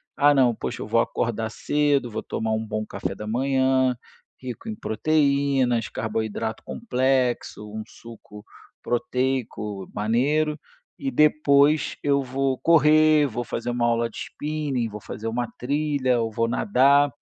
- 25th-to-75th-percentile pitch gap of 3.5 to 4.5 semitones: Yes, average, 4.1 semitones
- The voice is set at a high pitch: No, low, 130 Hz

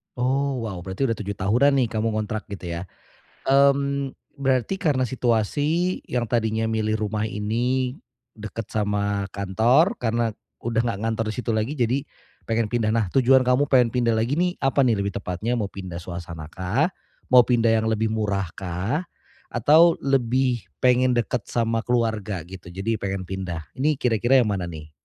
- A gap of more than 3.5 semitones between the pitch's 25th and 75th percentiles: Yes, average, 4.1 semitones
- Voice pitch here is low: Yes, low, 115 Hz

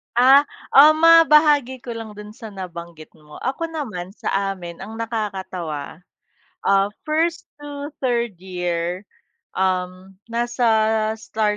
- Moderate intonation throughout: No, wide, 6.7 semitones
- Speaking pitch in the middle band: No, high, 215 Hz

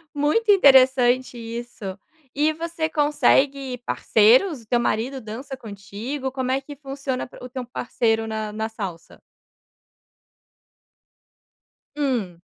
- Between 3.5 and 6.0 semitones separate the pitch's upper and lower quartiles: Yes, average, 4.0 semitones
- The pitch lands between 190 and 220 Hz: No, very high, 255 Hz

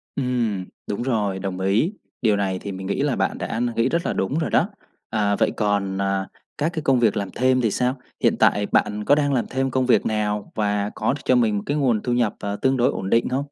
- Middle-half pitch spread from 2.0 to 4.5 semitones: Yes, average, 4.2 semitones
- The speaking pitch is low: Yes, low, 110 Hz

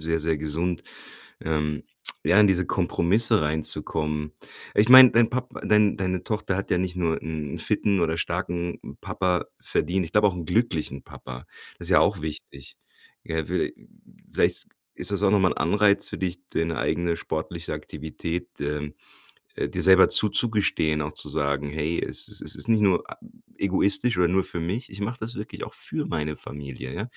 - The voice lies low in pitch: Yes, very low, 90 Hz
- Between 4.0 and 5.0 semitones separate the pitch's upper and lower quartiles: Yes, average, 4.4 semitones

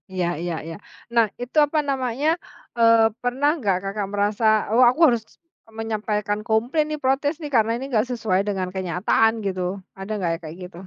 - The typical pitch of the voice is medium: No, high, 225 Hz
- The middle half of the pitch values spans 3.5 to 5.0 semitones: Yes, average, 4.5 semitones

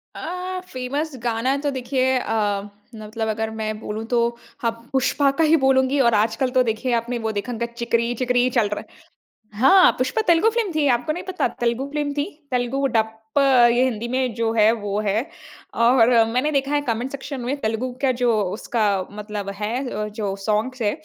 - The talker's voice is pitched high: Yes, high, 240 Hz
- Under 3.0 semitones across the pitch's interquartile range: No, average, 3.3 semitones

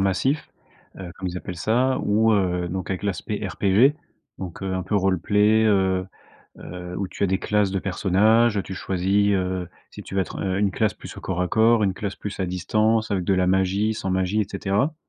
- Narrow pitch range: Yes, narrow, 2.3 semitones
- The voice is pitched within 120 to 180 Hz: No, very low, 95 Hz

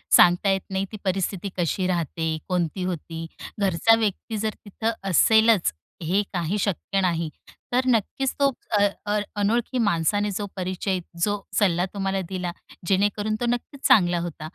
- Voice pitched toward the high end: Yes, high, 195 Hz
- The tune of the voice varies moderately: Yes, average, 3.2 semitones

